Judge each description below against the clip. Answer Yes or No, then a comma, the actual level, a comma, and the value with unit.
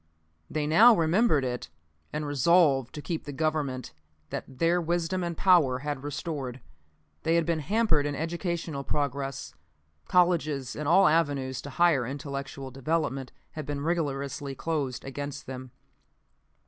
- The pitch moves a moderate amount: Yes, average, 3.5 semitones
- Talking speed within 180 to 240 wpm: No, slow, 135 wpm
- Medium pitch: Yes, medium, 145 Hz